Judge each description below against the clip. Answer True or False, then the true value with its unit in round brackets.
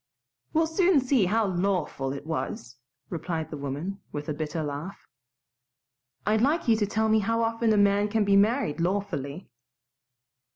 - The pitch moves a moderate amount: False (6.2 semitones)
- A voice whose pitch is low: False (200 Hz)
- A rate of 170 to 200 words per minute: False (160 wpm)